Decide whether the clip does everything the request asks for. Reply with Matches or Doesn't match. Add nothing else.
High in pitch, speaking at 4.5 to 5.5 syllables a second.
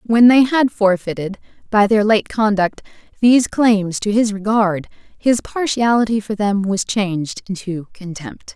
Doesn't match